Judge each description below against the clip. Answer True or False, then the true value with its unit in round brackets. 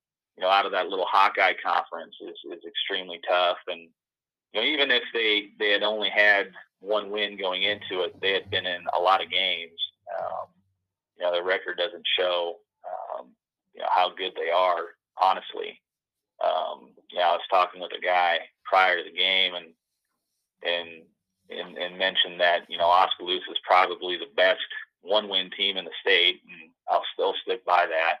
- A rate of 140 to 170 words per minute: False (185 wpm)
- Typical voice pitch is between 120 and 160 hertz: False (100 Hz)